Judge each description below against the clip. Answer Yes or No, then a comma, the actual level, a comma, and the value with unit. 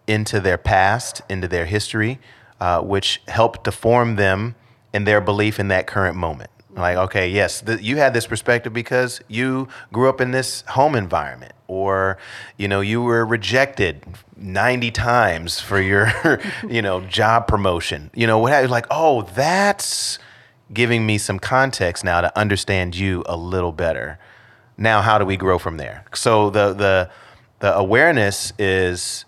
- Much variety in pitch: No, average, 3.7 semitones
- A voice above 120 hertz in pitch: No, low, 105 Hz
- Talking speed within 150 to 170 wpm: Yes, average, 165 wpm